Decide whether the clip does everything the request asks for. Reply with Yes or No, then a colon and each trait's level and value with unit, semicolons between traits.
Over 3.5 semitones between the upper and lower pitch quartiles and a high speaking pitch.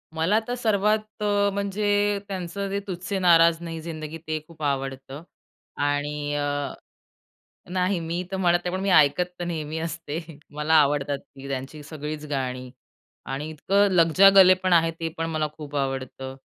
No: average, 4.2 semitones; medium, 165 Hz